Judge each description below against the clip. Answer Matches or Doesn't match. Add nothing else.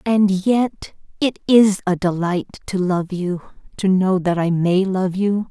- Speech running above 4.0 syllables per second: Doesn't match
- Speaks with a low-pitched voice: Doesn't match